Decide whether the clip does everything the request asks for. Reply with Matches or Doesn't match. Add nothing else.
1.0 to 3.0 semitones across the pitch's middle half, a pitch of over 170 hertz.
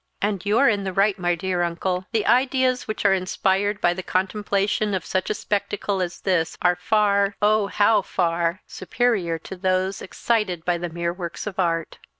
Matches